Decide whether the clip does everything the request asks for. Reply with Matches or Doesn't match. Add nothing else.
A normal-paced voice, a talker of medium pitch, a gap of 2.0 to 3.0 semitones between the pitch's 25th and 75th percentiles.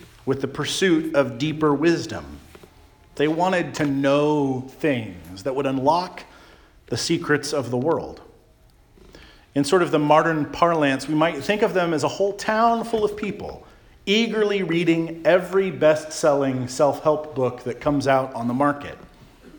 Doesn't match